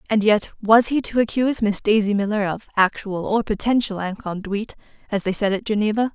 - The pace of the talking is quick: No, average, 185 wpm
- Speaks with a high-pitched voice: Yes, high, 210 Hz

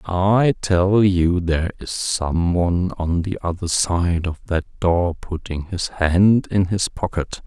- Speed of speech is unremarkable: Yes, average, 160 wpm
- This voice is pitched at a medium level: No, very low, 90 Hz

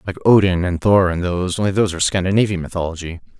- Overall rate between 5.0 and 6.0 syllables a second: No, 7.3 syllables/s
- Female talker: No, male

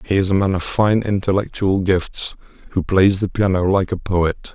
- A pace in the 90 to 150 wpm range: No, average, 200 wpm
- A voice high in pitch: No, very low, 95 Hz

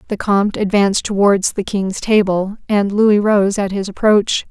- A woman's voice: Yes, female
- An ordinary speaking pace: Yes, average, 175 wpm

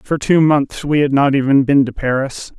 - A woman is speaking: No, male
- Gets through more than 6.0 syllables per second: No, 4.8 syllables/s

